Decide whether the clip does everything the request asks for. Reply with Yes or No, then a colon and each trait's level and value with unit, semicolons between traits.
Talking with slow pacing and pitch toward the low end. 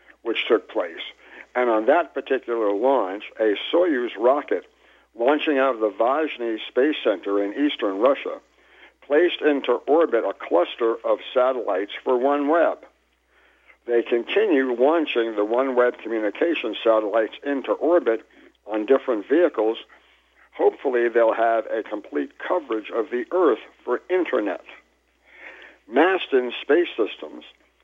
Yes: slow, 120 wpm; low, 130 Hz